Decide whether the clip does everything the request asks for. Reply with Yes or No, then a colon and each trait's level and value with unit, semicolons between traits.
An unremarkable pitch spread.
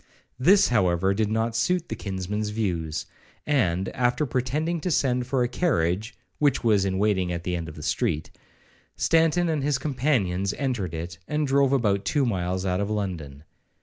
No: wide, 7.0 semitones